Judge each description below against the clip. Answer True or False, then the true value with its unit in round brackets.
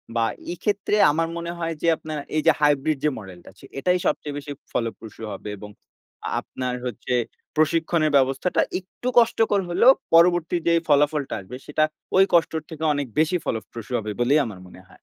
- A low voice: False (150 Hz)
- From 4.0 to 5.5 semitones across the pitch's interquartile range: True (5.2 semitones)